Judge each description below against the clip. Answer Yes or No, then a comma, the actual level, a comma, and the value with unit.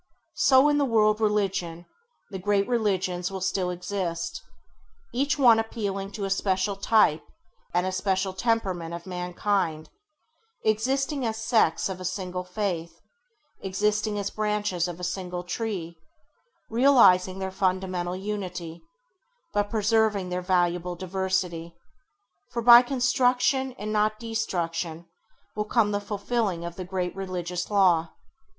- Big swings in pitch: No, average, 3.2 semitones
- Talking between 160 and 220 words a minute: No, slow, 135 wpm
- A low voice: No, high, 195 Hz